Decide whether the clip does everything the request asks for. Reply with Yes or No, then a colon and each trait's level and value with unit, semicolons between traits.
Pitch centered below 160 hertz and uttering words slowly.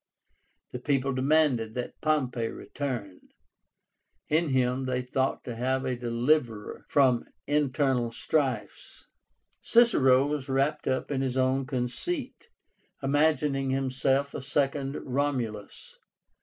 Yes: low, 135 Hz; slow, 110 wpm